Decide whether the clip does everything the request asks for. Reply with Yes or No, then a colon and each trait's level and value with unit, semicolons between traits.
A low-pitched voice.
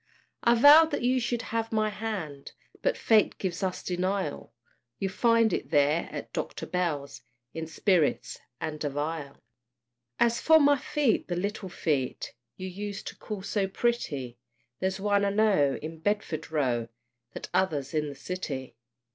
No: medium, 185 Hz